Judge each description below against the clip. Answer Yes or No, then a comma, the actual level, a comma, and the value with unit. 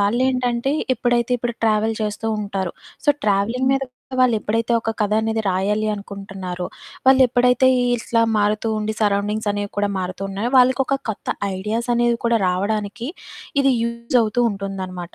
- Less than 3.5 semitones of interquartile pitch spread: Yes, average, 3.1 semitones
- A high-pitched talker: Yes, high, 220 Hz